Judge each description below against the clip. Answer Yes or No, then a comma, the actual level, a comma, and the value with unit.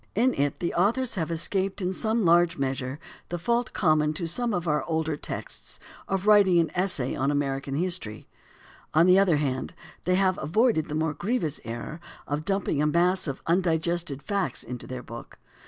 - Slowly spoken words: No, average, 175 wpm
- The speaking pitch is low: No, medium, 170 Hz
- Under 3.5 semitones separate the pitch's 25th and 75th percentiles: No, average, 4.4 semitones